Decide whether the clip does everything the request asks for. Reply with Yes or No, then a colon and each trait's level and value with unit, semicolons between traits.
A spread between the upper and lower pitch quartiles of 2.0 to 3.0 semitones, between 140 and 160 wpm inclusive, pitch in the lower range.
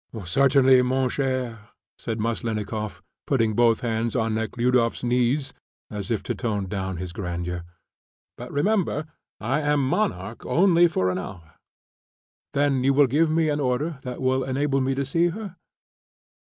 No: average, 4.5 semitones; average, 150 wpm; low, 125 Hz